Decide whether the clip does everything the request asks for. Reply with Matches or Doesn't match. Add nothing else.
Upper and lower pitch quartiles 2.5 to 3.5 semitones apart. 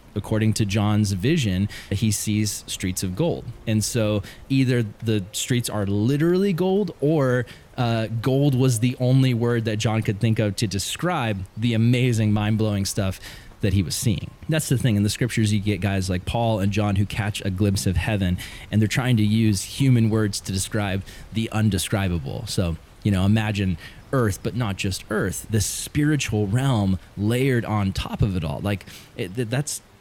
Matches